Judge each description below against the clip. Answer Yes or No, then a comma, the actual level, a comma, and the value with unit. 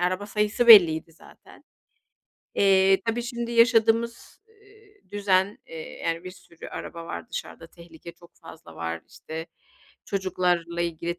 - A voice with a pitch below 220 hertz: Yes, medium, 185 Hz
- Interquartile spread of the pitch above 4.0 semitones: Yes, average, 5.0 semitones